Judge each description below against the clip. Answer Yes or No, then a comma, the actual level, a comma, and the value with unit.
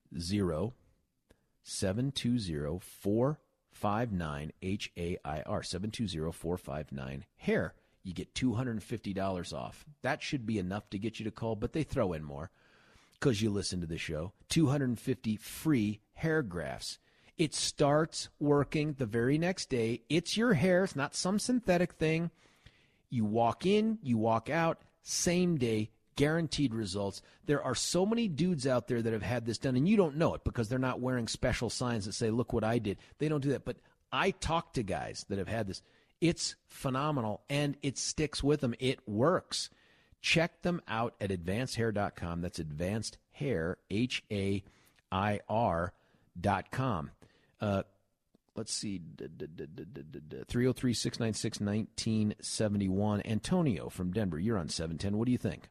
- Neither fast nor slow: Yes, average, 165 wpm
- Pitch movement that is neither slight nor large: No, wide, 5.9 semitones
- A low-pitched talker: Yes, low, 115 Hz